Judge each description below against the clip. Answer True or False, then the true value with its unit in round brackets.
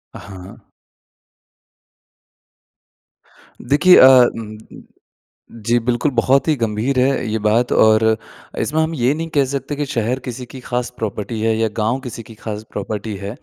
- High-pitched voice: False (120 Hz)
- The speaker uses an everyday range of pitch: True (3.5 semitones)